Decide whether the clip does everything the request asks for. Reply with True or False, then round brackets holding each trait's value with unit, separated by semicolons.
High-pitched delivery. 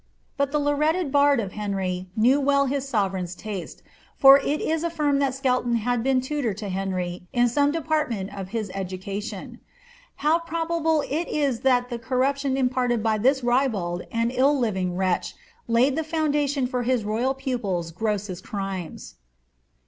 True (250 Hz)